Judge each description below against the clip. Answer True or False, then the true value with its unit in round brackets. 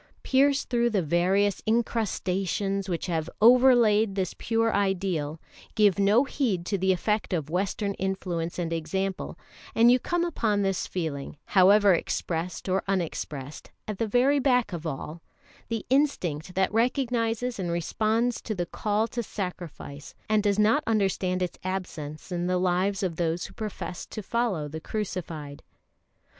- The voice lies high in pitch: True (195 Hz)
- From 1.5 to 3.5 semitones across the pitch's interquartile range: False (4.3 semitones)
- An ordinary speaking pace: True (150 wpm)